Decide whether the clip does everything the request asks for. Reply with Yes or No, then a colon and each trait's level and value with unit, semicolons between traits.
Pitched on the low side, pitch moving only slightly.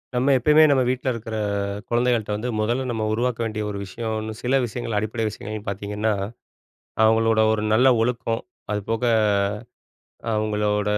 Yes: low, 110 Hz; narrow, 2.2 semitones